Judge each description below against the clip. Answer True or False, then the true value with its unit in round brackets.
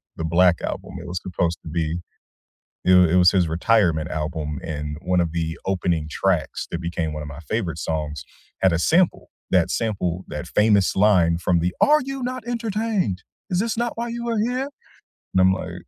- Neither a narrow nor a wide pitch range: False (5.7 semitones)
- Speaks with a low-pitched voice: True (90 Hz)